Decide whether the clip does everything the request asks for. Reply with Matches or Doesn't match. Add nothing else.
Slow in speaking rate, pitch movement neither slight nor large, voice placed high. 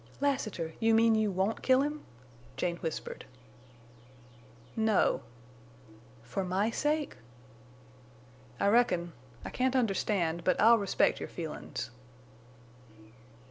Matches